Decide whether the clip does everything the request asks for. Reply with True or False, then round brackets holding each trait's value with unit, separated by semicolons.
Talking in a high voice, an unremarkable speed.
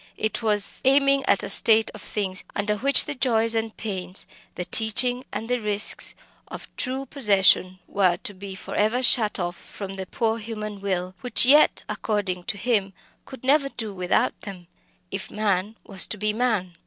True (210 Hz; 180 wpm)